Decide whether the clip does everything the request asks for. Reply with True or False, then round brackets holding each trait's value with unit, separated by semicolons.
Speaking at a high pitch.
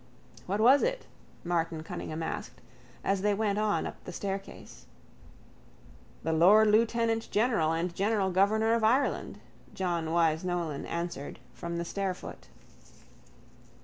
True (195 Hz)